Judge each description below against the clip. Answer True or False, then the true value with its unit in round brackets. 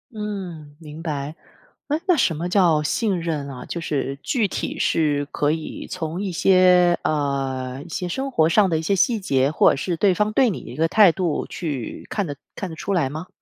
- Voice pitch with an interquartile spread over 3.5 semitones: True (4.4 semitones)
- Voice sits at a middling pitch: True (165 Hz)